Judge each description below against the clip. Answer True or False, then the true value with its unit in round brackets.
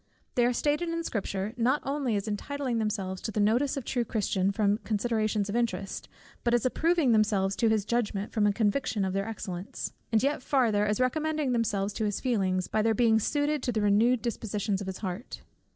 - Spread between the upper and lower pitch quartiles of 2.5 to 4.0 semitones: True (3.5 semitones)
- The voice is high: True (220 Hz)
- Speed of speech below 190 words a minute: False (205 wpm)